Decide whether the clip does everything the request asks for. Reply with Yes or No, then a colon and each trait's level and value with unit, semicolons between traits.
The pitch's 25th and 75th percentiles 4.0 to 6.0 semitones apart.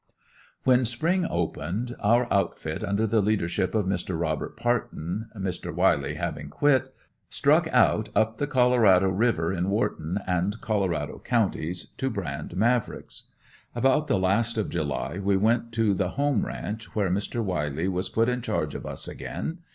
Yes: average, 4.7 semitones